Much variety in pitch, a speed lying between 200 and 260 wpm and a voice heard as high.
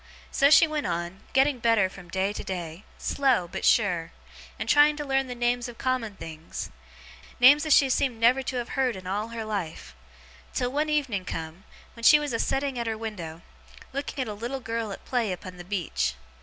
Yes: wide, 6.1 semitones; fast, 205 wpm; high, 230 Hz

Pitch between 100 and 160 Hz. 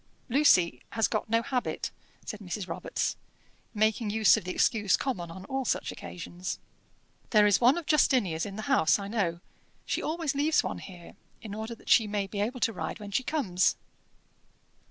No: high, 215 Hz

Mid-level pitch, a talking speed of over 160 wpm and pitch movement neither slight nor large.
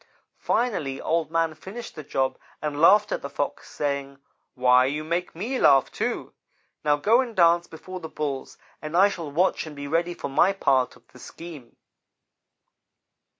Yes: medium, 160 Hz; average, 170 wpm; average, 4.1 semitones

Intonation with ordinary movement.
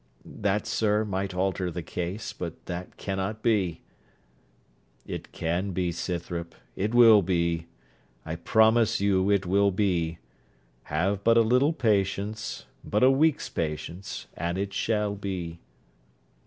Yes: average, 3.5 semitones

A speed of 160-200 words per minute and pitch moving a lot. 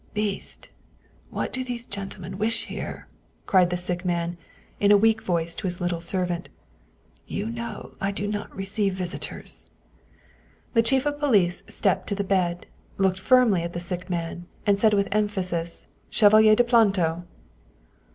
No: average, 170 wpm; average, 3.4 semitones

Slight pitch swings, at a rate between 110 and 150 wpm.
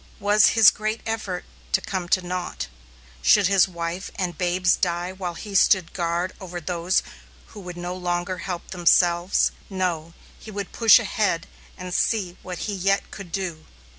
No: narrow, 2.0 semitones; average, 165 wpm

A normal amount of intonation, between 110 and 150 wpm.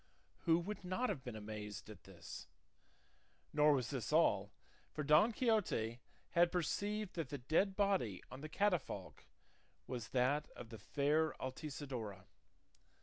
No: wide, 7.4 semitones; average, 140 wpm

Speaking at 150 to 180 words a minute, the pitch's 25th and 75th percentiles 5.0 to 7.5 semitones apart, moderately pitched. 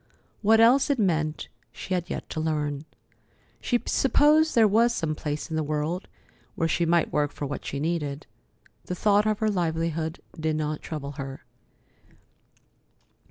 Yes: average, 160 wpm; wide, 5.5 semitones; medium, 165 Hz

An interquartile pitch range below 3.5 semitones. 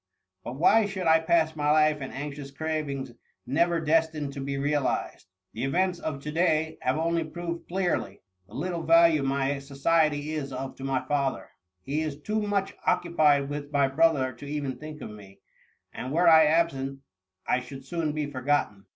Yes: average, 3.1 semitones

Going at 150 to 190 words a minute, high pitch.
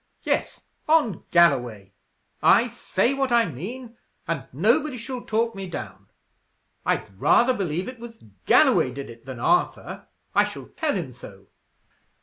No: average, 140 wpm; high, 195 Hz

